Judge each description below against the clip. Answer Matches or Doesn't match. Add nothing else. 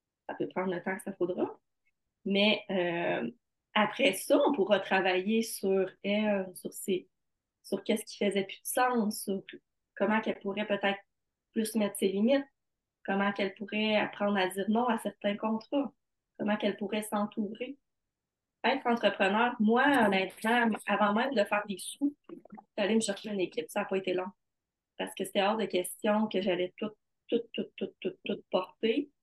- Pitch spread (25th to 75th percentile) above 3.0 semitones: Doesn't match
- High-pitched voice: Matches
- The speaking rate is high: Doesn't match